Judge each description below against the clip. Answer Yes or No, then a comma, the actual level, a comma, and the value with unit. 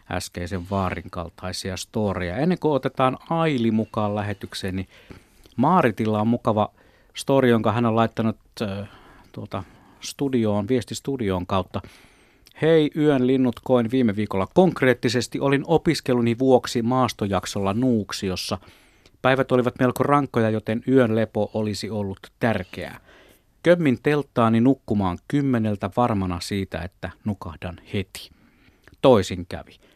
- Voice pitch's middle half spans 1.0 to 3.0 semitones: No, average, 4.7 semitones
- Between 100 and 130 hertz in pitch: Yes, low, 110 Hz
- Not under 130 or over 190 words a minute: No, average, 115 wpm